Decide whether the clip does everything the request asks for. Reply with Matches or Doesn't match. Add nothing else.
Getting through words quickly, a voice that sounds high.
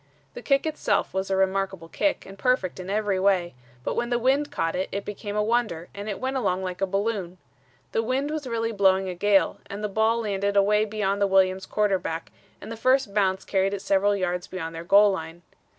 Matches